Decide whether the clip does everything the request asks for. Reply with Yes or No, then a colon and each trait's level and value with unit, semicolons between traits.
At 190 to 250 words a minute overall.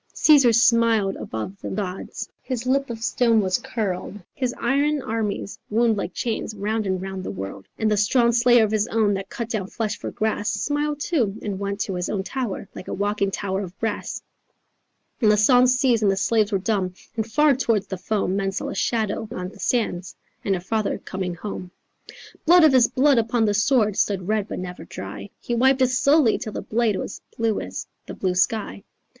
Yes: fast, 205 wpm